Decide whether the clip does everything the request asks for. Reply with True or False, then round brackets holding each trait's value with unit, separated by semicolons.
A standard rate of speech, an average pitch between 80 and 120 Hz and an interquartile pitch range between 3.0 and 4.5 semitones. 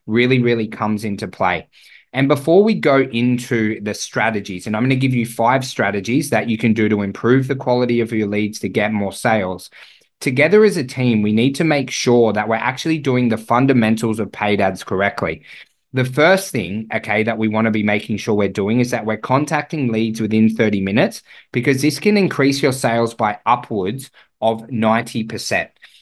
True (195 wpm; 115 Hz; 3.4 semitones)